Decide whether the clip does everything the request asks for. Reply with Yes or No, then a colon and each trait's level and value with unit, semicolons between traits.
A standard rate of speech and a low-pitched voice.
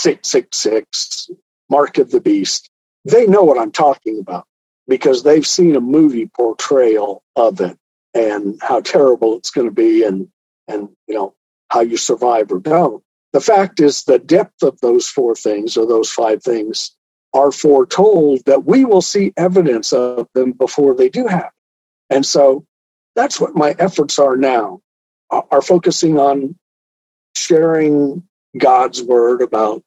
No: average, 155 wpm; medium, 150 Hz